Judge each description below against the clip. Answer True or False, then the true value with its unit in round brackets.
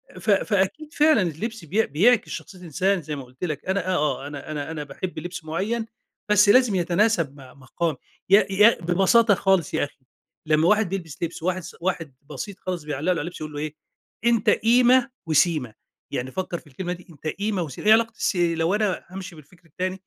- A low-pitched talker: False (180 Hz)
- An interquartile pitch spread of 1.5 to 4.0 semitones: False (4.7 semitones)